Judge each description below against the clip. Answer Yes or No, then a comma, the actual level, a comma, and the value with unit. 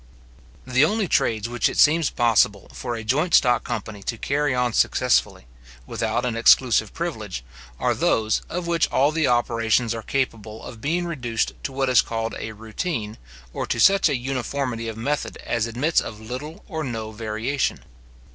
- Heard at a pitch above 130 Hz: No, low, 120 Hz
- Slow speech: No, average, 170 wpm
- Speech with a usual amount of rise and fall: Yes, average, 4.3 semitones